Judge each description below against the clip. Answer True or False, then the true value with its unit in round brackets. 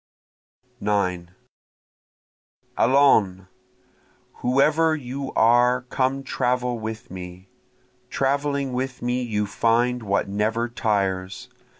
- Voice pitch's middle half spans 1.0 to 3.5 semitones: False (4.4 semitones)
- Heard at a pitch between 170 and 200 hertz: False (120 Hz)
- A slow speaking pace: True (85 wpm)